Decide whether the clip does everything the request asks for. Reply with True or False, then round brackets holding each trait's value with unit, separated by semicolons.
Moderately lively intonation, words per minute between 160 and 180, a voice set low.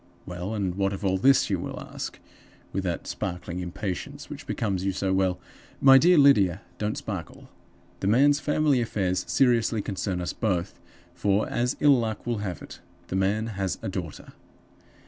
True (4.1 semitones; 175 wpm; 100 Hz)